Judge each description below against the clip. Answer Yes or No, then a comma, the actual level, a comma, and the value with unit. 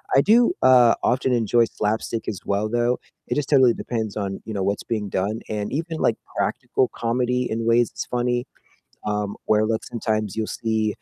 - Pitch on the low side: Yes, low, 115 Hz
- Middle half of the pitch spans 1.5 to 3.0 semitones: Yes, narrow, 2.5 semitones